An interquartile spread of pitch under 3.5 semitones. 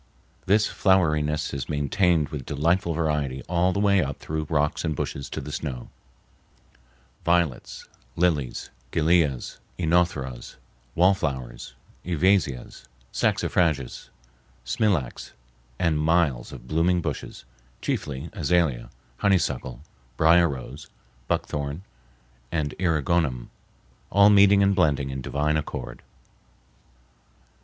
No: average, 4.4 semitones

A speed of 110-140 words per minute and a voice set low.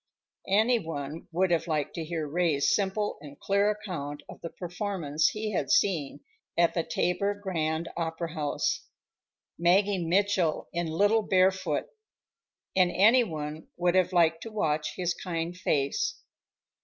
No: slow, 135 wpm; medium, 175 Hz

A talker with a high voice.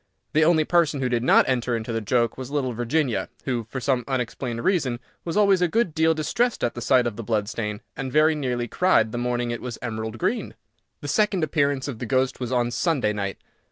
No: low, 130 Hz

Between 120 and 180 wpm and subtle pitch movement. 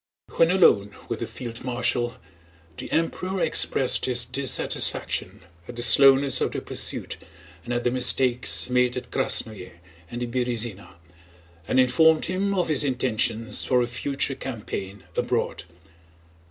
Yes: average, 140 wpm; narrow, 2.3 semitones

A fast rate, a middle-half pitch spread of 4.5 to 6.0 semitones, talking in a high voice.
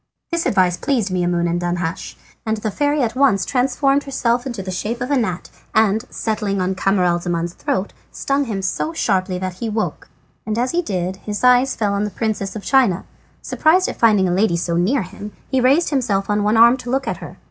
Yes: fast, 210 wpm; average, 5.2 semitones; high, 210 Hz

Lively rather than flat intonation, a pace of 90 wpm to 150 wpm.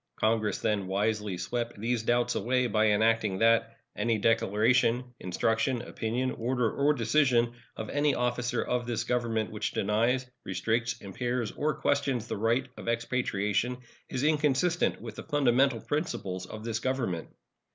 No: narrow, 2.6 semitones; average, 140 wpm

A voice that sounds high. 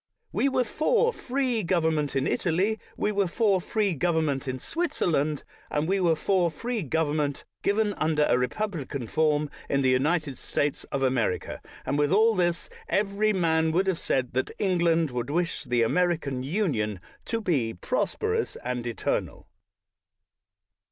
No: medium, 165 Hz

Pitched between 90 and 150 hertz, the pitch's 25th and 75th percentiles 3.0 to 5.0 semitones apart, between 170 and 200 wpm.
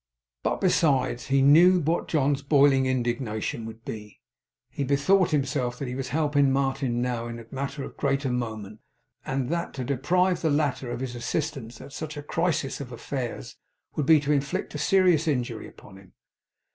Yes: low, 135 Hz; average, 3.4 semitones; average, 180 wpm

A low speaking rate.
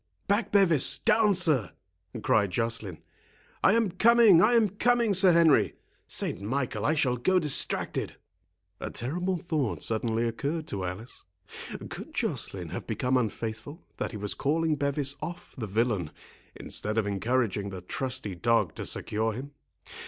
No: average, 145 wpm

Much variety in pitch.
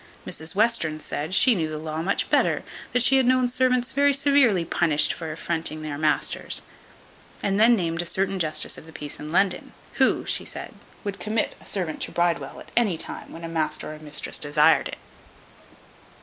Yes: wide, 6.7 semitones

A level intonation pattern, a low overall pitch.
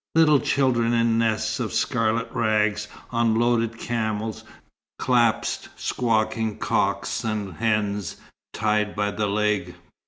Yes: narrow, 1.7 semitones; low, 110 Hz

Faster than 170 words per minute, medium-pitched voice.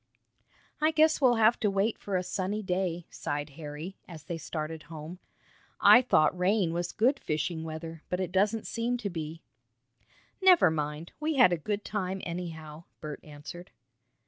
No: average, 165 wpm; medium, 180 Hz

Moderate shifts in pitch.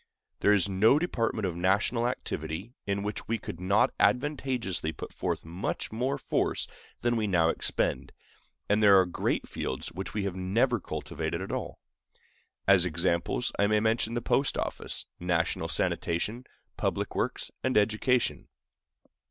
Yes: average, 4.4 semitones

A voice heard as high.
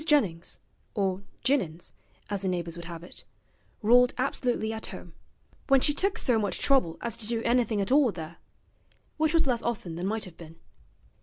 Yes: high, 220 Hz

